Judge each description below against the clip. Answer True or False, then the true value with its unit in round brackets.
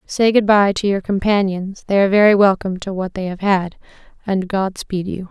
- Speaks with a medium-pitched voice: False (195 Hz)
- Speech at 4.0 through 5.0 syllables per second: False (5.3 syllables/s)